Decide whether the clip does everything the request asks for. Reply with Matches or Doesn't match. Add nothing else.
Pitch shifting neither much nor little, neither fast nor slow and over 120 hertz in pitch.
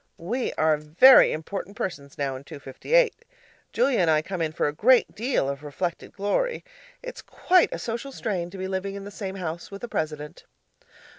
Doesn't match